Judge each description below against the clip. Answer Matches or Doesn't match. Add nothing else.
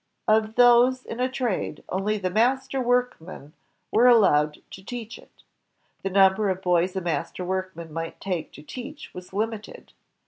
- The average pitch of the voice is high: Matches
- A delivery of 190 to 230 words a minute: Doesn't match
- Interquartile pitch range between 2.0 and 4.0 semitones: Doesn't match